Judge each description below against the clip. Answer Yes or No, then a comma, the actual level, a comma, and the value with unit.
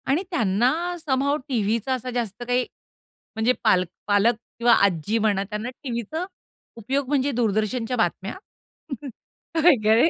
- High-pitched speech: Yes, high, 235 Hz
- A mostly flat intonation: No, average, 3.7 semitones